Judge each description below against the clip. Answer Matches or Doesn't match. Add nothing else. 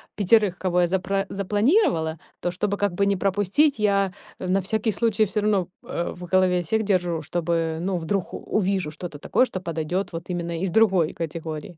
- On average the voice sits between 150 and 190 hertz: Matches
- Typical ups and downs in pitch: Matches